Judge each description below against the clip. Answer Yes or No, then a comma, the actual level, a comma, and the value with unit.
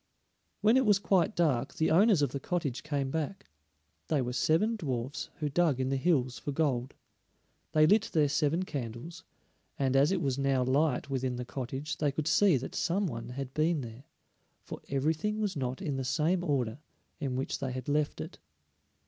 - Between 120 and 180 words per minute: No, average, 190 wpm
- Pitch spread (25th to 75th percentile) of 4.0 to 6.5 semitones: Yes, average, 4.3 semitones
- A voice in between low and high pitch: Yes, medium, 145 Hz